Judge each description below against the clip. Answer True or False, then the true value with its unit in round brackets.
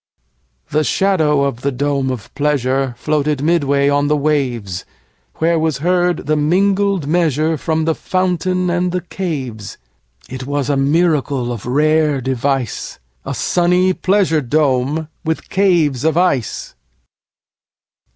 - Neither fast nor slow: False (110 wpm)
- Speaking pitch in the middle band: True (150 Hz)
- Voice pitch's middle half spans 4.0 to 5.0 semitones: True (4.3 semitones)